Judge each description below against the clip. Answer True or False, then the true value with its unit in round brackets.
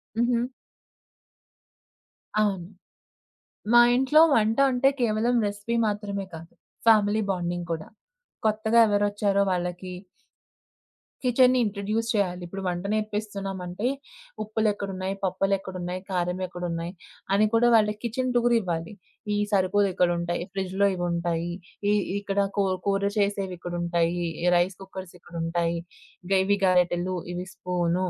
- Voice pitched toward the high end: True (195 Hz)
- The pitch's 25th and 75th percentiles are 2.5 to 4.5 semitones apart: True (3.2 semitones)